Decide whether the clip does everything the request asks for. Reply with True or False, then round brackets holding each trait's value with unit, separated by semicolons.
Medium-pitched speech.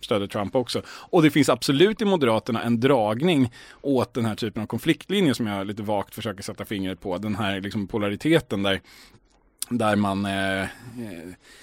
False (110 Hz)